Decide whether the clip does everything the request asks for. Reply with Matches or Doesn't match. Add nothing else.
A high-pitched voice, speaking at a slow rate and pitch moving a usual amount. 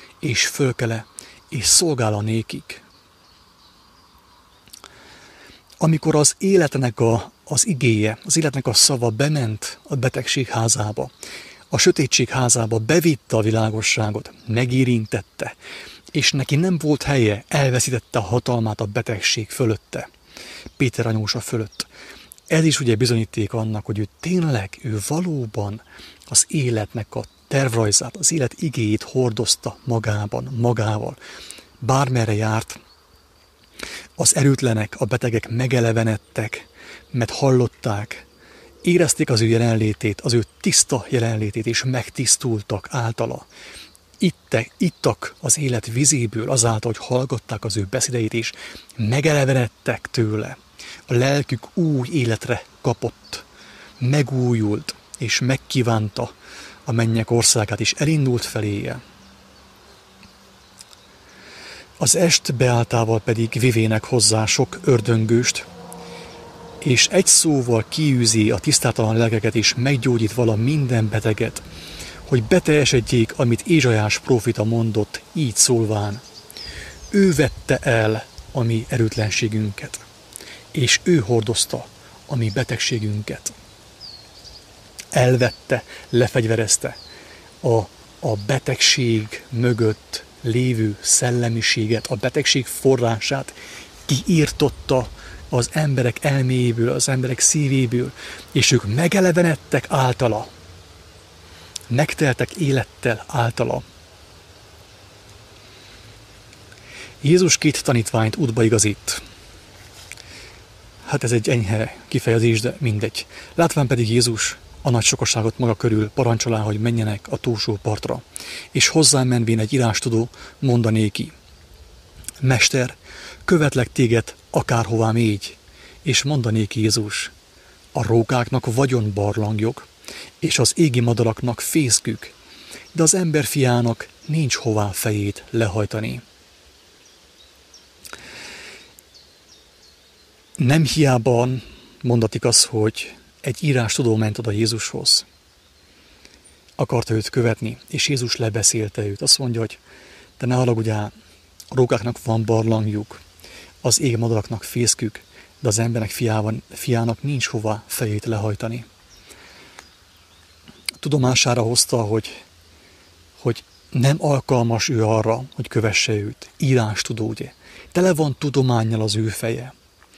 Doesn't match